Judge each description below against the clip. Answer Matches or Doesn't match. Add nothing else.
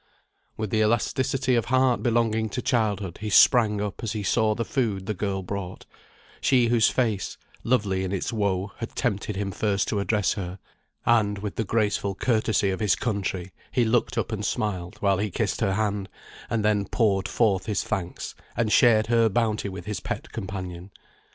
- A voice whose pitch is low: Matches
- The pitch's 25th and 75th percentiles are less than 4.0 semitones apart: Matches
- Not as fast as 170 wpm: Doesn't match